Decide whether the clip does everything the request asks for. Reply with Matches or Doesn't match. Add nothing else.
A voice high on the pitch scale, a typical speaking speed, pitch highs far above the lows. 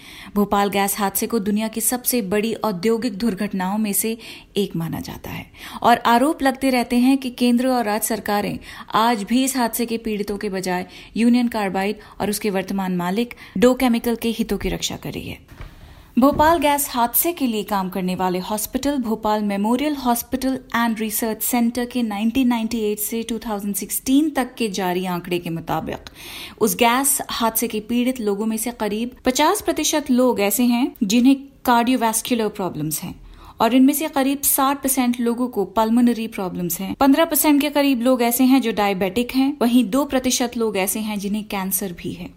Doesn't match